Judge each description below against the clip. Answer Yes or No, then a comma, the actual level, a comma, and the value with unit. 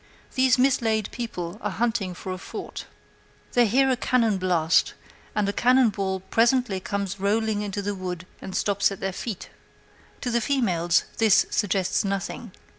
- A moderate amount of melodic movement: Yes, average, 3.8 semitones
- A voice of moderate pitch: No, high, 205 Hz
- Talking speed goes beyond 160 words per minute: No, average, 155 wpm